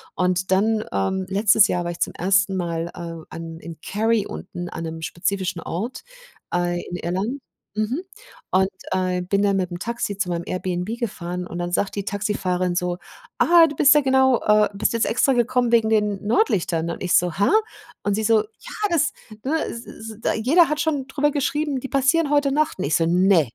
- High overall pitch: Yes, high, 200 Hz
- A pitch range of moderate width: No, wide, 5.7 semitones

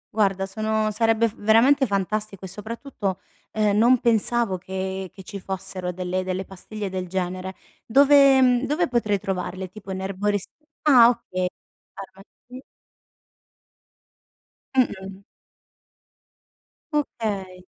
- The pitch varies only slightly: No, average, 3.6 semitones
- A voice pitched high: Yes, high, 205 Hz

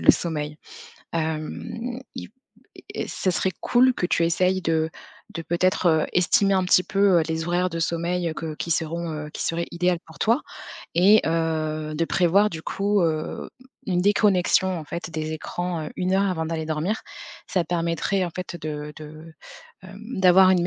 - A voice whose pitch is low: No, medium, 170 Hz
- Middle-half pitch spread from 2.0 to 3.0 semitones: Yes, narrow, 2.6 semitones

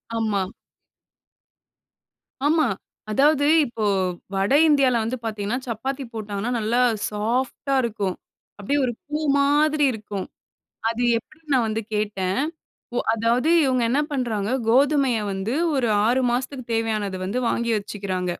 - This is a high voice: Yes, high, 235 Hz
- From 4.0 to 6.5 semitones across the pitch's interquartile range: Yes, average, 4.3 semitones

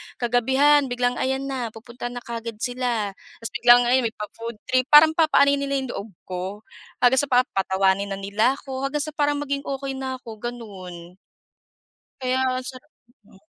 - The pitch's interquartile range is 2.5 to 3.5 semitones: Yes, average, 3.2 semitones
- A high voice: Yes, high, 245 Hz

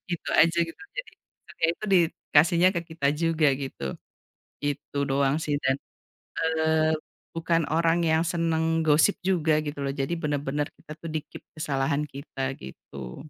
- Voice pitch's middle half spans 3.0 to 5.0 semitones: No, narrow, 2.6 semitones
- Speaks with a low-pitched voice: No, medium, 155 Hz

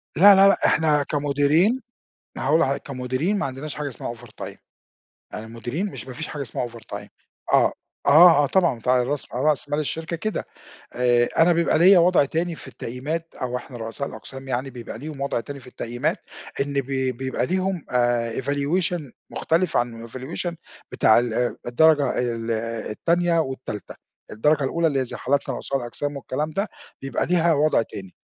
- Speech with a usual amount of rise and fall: Yes, average, 4.7 semitones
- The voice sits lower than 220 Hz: Yes, medium, 140 Hz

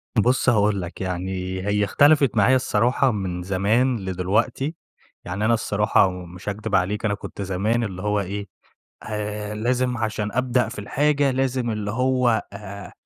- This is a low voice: Yes, low, 105 Hz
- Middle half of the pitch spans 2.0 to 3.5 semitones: No, average, 3.9 semitones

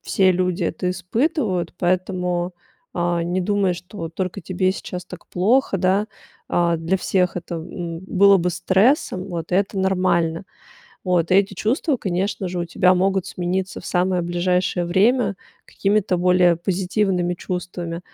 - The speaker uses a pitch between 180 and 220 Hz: Yes, medium, 185 Hz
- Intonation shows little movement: Yes, narrow, 1.7 semitones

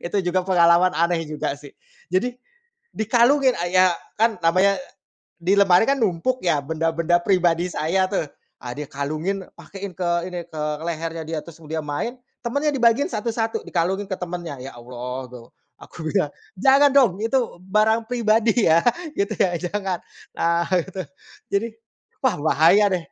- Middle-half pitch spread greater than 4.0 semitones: Yes, average, 4.7 semitones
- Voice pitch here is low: No, medium, 185 Hz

